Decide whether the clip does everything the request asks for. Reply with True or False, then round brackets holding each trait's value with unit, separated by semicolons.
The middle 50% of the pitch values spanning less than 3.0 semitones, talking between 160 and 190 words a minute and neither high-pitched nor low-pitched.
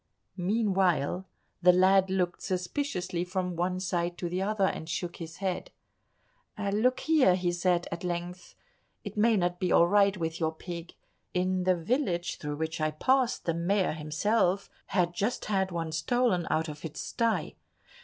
True (2.5 semitones; 165 wpm; 180 Hz)